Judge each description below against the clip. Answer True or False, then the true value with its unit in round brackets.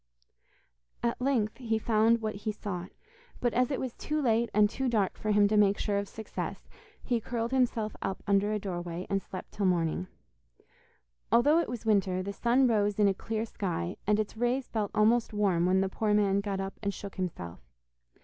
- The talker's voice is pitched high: True (210 Hz)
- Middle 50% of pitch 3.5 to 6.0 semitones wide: False (3.0 semitones)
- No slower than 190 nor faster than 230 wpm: True (195 wpm)